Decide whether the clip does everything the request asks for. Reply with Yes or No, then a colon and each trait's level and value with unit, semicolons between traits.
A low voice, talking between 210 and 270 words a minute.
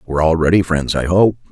Yes: very low, 85 Hz; fast, 240 wpm